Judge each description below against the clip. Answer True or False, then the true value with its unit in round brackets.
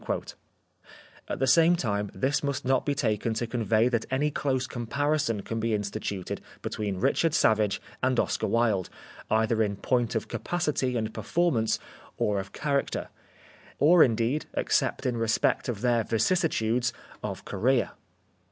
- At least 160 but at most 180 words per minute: False (150 wpm)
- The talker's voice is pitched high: False (120 Hz)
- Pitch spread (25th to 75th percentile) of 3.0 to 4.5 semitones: True (4.1 semitones)